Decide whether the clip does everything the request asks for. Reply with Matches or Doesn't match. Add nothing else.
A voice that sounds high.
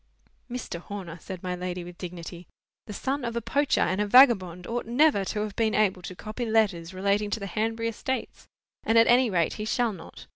Matches